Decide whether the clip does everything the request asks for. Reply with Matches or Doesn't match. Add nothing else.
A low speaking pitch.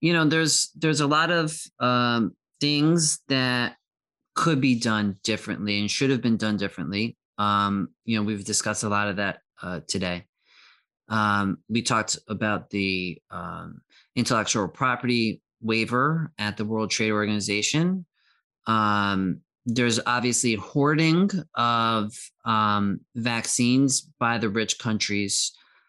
Matches